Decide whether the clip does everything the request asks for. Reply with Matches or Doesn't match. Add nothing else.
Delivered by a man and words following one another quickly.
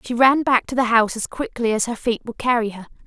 Doesn't match